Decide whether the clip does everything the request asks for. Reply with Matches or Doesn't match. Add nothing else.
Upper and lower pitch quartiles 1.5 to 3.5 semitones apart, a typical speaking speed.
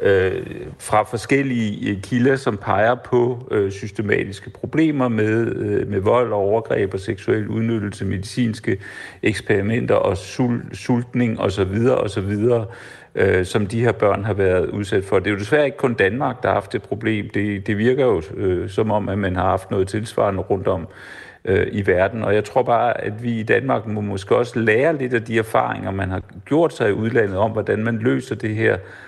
Matches